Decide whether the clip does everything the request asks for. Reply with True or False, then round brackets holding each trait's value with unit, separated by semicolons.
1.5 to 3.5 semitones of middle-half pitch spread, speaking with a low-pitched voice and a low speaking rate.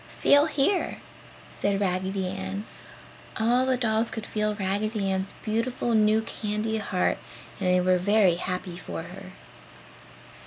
False (2.7 semitones; 210 Hz; 130 wpm)